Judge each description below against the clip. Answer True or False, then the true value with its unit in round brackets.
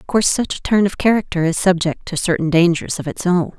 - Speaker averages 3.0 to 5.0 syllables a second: False (6.0 syllables/s)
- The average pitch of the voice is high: False (180 Hz)